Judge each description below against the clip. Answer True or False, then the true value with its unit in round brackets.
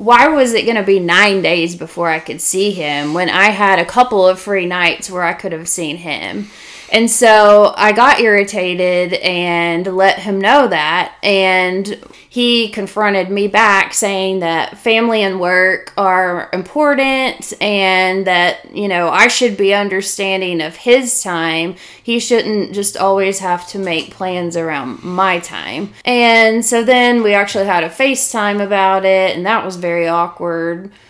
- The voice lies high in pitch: True (195 Hz)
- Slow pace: False (165 wpm)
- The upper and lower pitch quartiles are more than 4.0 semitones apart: False (3.2 semitones)